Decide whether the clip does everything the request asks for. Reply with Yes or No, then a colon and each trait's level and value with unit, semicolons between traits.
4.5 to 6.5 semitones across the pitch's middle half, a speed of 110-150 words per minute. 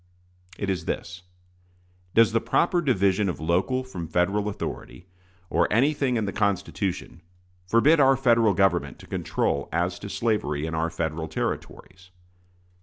Yes: average, 5.0 semitones; average, 140 wpm